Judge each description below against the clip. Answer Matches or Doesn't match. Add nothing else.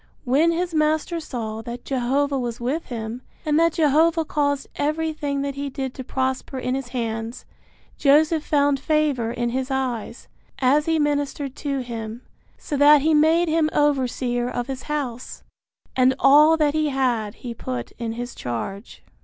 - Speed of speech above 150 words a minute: Matches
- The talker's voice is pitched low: Doesn't match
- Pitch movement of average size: Matches